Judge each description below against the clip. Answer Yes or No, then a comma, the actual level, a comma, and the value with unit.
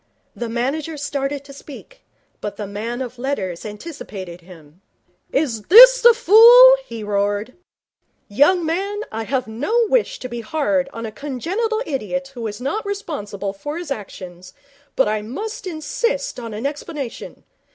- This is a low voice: No, very high, 270 Hz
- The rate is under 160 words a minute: Yes, average, 150 wpm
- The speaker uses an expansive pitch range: Yes, wide, 8.1 semitones